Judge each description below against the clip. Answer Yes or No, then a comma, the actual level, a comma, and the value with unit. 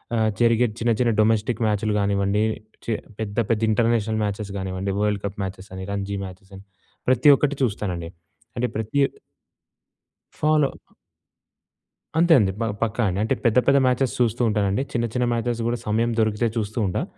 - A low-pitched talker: Yes, low, 110 Hz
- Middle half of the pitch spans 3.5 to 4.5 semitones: No, average, 2.9 semitones